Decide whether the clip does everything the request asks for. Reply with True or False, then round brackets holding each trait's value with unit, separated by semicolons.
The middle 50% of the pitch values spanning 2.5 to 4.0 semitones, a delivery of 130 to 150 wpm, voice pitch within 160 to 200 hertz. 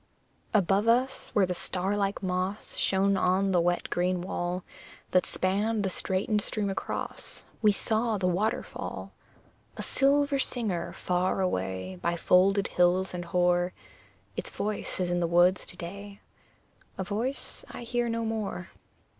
True (2.9 semitones; 145 wpm; 190 Hz)